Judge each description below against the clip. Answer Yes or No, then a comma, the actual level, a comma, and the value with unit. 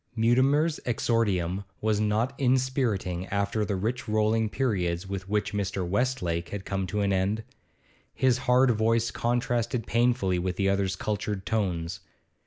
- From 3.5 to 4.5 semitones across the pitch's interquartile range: Yes, average, 3.9 semitones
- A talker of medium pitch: No, low, 105 Hz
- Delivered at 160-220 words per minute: No, average, 140 wpm